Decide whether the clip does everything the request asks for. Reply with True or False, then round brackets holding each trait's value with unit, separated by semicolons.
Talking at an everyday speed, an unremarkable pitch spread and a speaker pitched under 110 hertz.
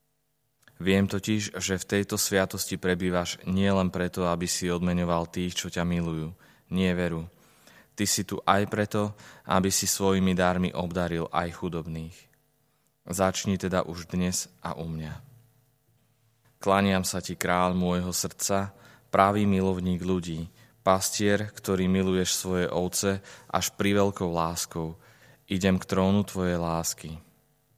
False (130 wpm; 2.2 semitones; 95 Hz)